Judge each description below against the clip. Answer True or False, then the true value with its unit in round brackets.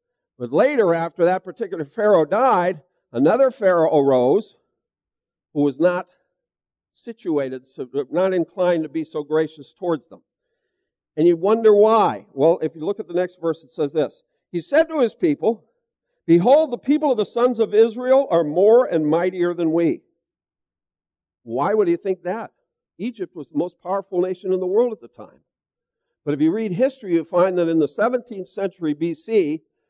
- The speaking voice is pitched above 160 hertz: True (190 Hz)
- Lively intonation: True (7.1 semitones)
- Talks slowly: False (175 wpm)